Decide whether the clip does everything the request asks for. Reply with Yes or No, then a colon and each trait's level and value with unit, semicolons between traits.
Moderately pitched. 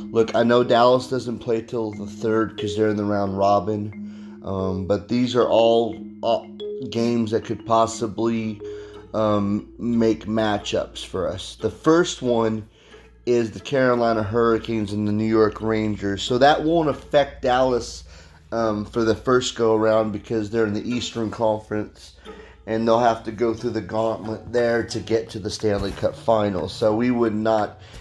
No: low, 110 Hz